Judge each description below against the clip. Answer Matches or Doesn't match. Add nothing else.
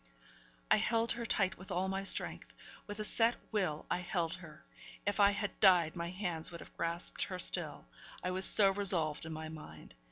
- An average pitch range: Matches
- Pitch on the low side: Doesn't match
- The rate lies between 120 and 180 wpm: Doesn't match